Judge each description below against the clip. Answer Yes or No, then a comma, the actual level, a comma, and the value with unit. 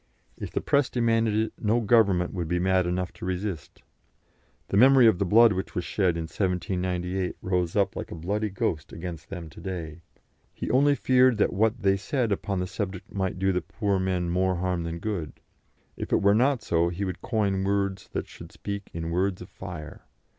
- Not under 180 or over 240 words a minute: Yes, average, 200 wpm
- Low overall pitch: Yes, very low, 95 Hz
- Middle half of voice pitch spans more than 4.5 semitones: No, average, 3.0 semitones